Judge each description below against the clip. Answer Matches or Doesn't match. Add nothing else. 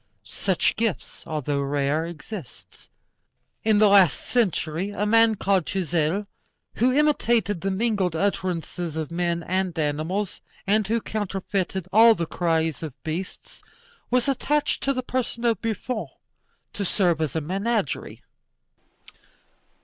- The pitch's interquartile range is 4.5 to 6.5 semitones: Matches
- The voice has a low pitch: Doesn't match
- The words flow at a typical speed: Doesn't match